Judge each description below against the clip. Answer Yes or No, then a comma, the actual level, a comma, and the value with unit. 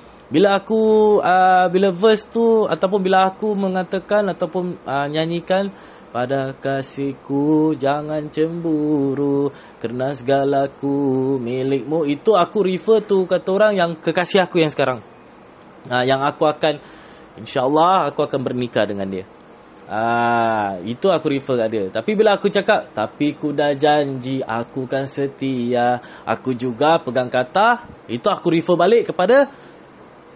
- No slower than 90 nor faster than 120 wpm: No, average, 135 wpm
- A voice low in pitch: No, medium, 150 Hz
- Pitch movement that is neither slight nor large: No, wide, 6.0 semitones